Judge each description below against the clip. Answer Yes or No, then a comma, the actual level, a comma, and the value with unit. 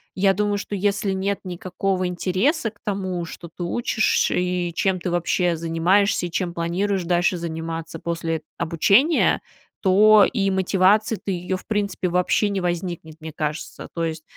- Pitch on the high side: No, medium, 180 Hz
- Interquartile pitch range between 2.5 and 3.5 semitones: Yes, average, 2.8 semitones